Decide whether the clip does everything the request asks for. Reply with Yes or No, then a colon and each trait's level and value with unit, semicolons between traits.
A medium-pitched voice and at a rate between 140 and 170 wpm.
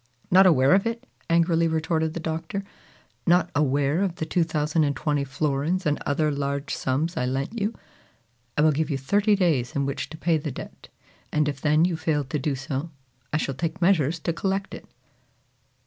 No: medium, 155 Hz; average, 180 wpm